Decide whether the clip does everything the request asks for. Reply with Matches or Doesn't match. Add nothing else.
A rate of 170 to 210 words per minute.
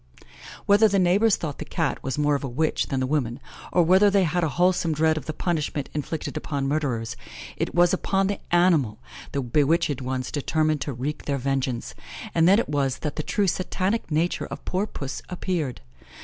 Matches